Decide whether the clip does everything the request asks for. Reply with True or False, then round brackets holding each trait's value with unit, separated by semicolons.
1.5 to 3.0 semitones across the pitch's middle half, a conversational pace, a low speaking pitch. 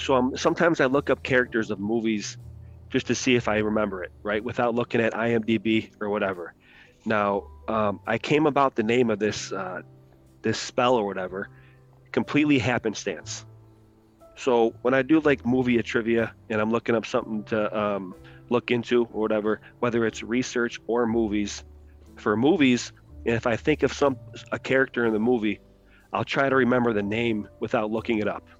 True (2.7 semitones; 175 wpm; 115 Hz)